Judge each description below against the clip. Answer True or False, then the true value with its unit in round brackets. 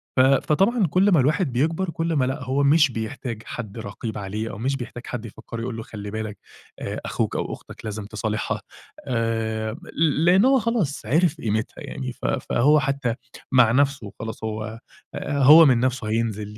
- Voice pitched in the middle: False (125 Hz)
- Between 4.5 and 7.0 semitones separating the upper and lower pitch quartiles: True (5.0 semitones)